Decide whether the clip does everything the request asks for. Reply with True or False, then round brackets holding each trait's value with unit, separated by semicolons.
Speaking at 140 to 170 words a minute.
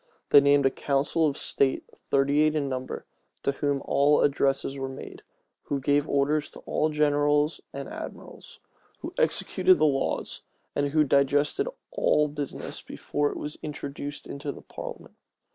True (150 wpm)